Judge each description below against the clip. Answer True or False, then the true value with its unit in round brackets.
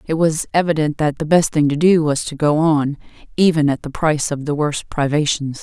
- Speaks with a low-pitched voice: False (150 Hz)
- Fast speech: True (225 wpm)